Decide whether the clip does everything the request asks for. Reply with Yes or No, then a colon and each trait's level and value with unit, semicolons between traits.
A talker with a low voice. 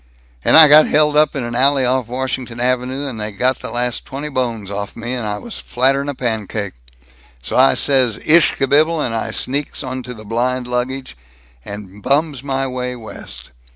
Yes: low, 125 Hz